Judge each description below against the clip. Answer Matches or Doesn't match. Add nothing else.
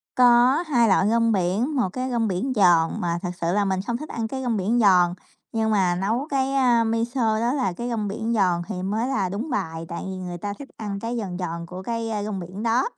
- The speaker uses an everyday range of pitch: Matches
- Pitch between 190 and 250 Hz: Matches